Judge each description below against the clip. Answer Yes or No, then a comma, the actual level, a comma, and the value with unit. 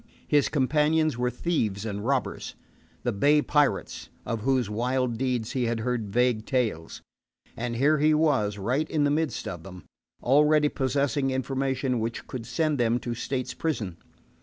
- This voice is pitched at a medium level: No, low, 130 Hz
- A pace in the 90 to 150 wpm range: No, average, 160 wpm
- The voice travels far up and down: No, average, 4.1 semitones